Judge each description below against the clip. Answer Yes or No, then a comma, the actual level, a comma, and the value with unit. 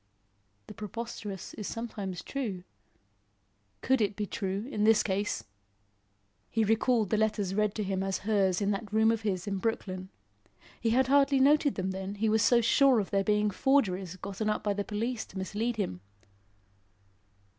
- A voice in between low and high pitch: No, high, 210 Hz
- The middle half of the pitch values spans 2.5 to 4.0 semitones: Yes, average, 2.8 semitones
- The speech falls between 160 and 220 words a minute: Yes, average, 170 wpm